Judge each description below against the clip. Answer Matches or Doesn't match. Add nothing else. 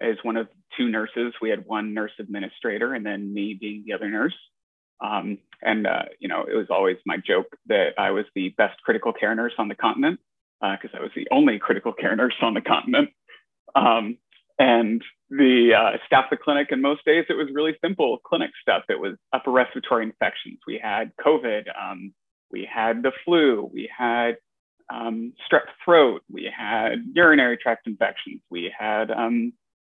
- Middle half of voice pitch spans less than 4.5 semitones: Doesn't match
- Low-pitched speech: Matches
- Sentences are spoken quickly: Doesn't match